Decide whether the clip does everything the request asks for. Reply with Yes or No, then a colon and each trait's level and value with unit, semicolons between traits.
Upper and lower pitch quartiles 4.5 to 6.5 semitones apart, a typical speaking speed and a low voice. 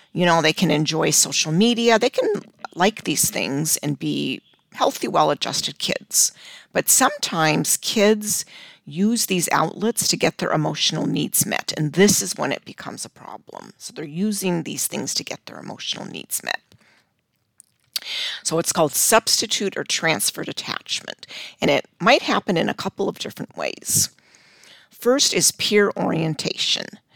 No: average, 5.0 semitones; average, 150 wpm; medium, 180 Hz